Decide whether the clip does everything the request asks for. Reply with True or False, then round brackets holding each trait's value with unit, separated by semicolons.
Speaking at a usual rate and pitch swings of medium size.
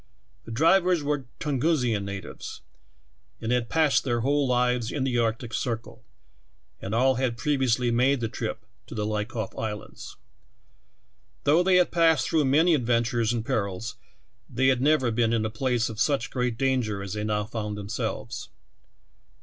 True (160 wpm; 3.6 semitones)